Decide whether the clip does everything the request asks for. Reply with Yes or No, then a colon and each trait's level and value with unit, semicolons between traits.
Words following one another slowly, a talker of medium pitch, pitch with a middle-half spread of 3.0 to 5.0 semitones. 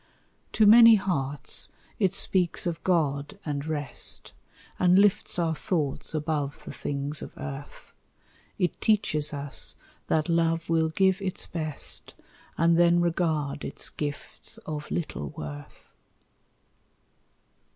Yes: slow, 120 wpm; medium, 160 Hz; average, 3.6 semitones